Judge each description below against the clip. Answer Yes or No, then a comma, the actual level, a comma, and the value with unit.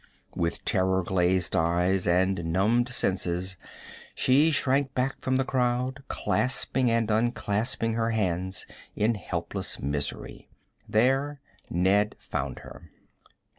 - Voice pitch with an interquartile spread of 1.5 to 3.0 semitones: No, wide, 5.6 semitones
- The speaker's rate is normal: No, slow, 110 wpm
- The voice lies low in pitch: Yes, low, 105 Hz